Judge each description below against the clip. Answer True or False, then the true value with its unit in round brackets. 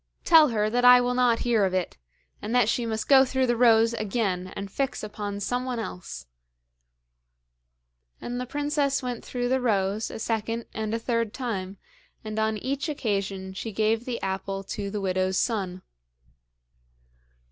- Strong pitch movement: False (3.7 semitones)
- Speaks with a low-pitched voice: False (225 Hz)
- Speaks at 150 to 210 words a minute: True (165 wpm)